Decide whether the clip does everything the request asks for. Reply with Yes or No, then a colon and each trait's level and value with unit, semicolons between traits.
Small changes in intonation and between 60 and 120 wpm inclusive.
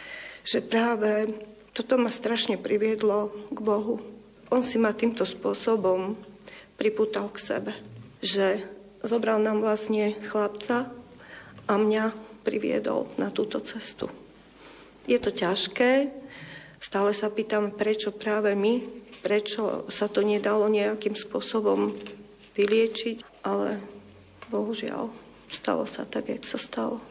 Yes: narrow, 1.7 semitones; average, 115 wpm